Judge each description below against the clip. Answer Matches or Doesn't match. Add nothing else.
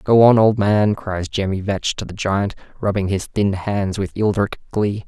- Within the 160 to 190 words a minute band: Doesn't match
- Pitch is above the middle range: Doesn't match